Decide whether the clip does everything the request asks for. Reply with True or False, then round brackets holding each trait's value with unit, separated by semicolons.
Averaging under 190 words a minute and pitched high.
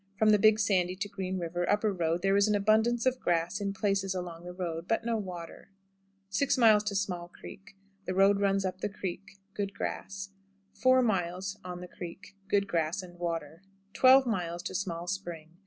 True (170 wpm; 195 Hz)